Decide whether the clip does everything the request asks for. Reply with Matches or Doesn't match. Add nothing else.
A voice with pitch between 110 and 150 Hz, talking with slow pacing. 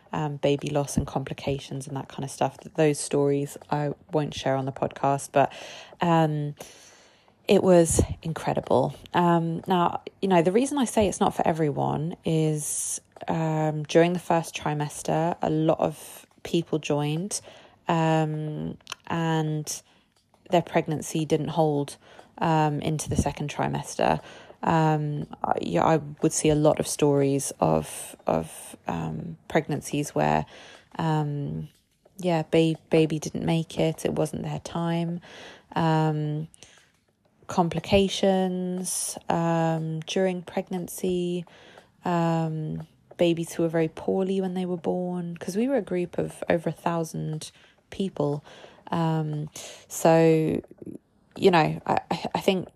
Doesn't match